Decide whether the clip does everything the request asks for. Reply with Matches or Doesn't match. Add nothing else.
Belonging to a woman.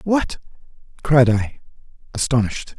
Doesn't match